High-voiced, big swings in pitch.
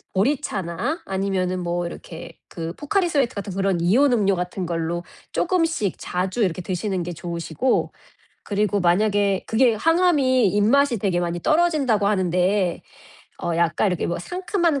Yes: high, 195 Hz; wide, 6.6 semitones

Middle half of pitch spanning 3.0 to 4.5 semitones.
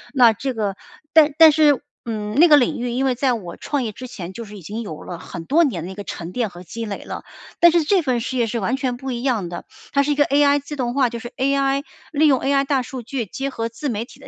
Yes: average, 4.2 semitones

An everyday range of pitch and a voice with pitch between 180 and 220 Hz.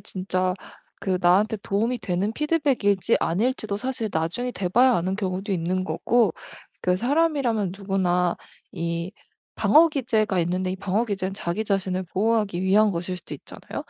Yes: average, 3.6 semitones; high, 195 Hz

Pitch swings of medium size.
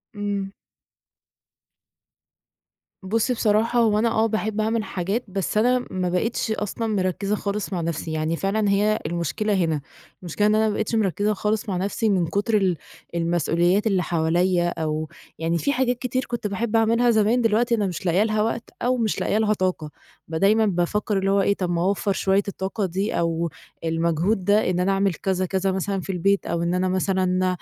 Yes: average, 3.3 semitones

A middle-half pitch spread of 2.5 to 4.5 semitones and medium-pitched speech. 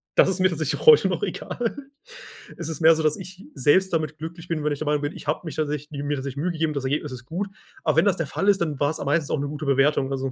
Yes: average, 2.8 semitones; medium, 155 Hz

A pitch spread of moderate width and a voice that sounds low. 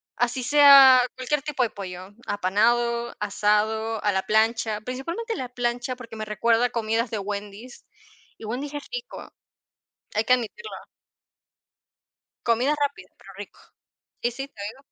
No: average, 3.3 semitones; high, 235 Hz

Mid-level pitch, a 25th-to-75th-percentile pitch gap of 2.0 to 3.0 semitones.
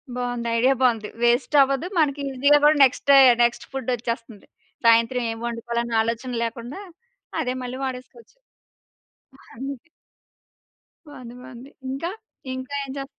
No: very high, 250 Hz; narrow, 2.5 semitones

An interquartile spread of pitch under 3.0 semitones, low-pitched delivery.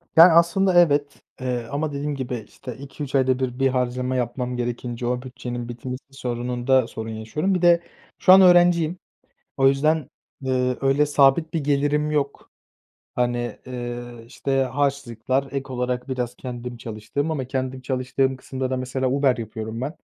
Yes: narrow, 2.6 semitones; low, 130 Hz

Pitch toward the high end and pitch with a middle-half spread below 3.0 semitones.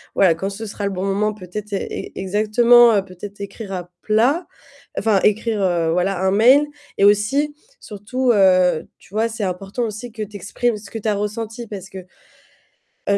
Yes: high, 205 Hz; narrow, 2.5 semitones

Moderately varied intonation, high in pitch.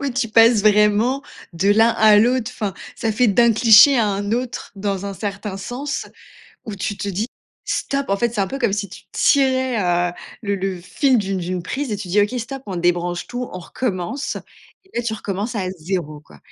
Yes: average, 3.9 semitones; high, 210 Hz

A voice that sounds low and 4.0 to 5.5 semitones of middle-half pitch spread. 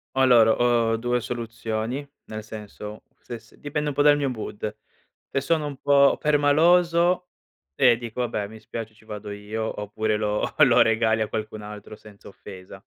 Yes: low, 115 Hz; average, 4.5 semitones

